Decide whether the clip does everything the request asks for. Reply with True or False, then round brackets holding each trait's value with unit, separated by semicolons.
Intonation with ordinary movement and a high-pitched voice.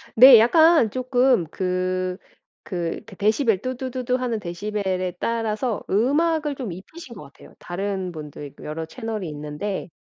False (5.7 semitones; 210 Hz)